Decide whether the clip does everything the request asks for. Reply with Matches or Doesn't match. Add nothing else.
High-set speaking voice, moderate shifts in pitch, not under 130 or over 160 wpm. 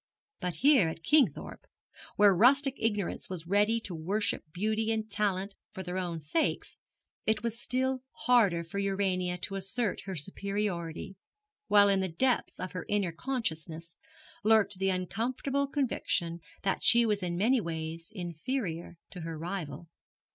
Matches